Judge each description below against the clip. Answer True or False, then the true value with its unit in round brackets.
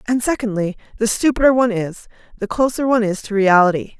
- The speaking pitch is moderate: False (220 Hz)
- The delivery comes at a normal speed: True (180 wpm)